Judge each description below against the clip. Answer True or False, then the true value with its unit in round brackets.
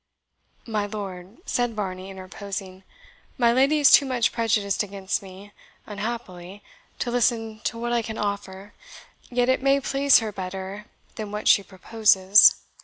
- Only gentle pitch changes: False (3.5 semitones)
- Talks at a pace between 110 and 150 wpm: True (145 wpm)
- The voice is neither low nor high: False (210 Hz)